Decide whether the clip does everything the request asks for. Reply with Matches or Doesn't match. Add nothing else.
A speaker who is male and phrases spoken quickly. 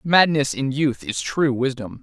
Doesn't match